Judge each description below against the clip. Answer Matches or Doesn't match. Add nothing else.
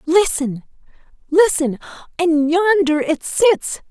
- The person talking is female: Matches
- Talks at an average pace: Doesn't match